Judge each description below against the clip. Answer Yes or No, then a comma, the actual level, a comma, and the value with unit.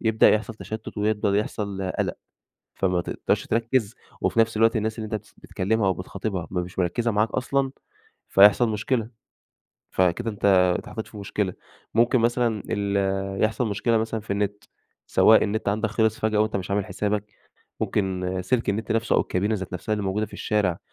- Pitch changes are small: Yes, narrow, 2.3 semitones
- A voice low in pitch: Yes, low, 105 Hz